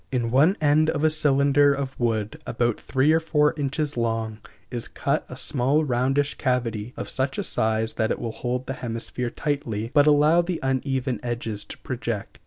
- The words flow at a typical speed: Yes, average, 185 wpm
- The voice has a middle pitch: No, low, 130 Hz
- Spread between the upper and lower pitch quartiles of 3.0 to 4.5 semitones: Yes, average, 3.7 semitones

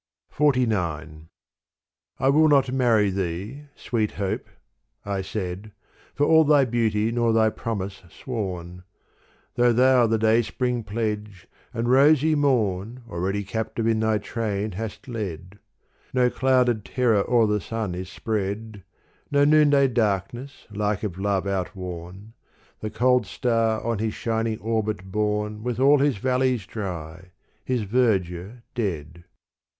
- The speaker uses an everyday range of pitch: Yes, average, 4.0 semitones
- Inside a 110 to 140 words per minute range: Yes, slow, 135 wpm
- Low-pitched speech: Yes, low, 110 Hz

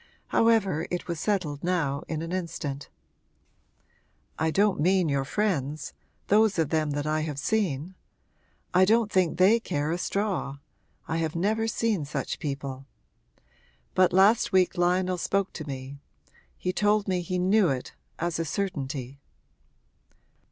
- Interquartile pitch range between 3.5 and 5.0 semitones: Yes, average, 4.7 semitones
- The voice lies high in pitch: No, medium, 175 Hz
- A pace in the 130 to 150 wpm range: Yes, average, 145 wpm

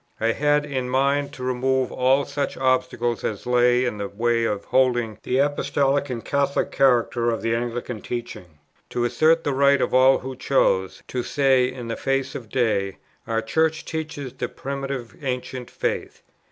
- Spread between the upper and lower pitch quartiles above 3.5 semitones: No, narrow, 2.6 semitones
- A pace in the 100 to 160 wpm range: No, average, 170 wpm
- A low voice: Yes, low, 130 Hz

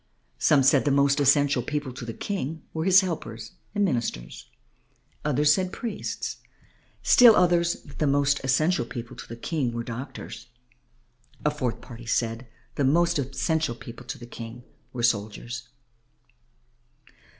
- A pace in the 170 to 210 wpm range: No, average, 150 wpm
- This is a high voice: No, low, 135 Hz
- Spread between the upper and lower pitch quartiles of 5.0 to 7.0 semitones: No, average, 4.5 semitones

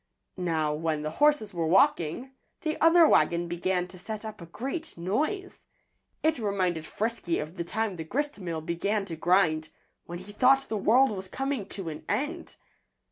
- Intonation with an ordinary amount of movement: No, wide, 7.3 semitones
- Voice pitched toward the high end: Yes, high, 195 Hz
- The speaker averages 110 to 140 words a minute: No, average, 170 wpm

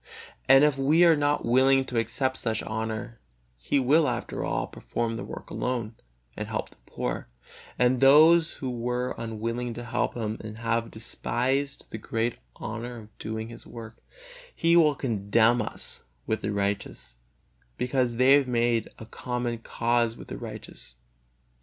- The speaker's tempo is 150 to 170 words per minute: Yes, average, 155 wpm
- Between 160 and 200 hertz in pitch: No, low, 120 Hz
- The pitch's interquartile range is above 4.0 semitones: No, average, 2.8 semitones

